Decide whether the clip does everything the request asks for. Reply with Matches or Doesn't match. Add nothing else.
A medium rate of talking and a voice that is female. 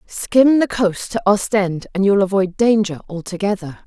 Matches